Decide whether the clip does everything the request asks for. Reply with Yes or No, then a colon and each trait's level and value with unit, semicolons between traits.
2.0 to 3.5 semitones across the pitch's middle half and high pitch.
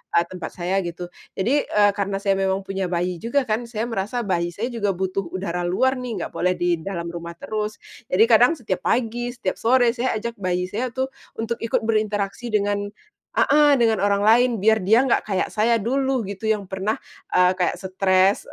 No: average, 3.9 semitones; high, 205 Hz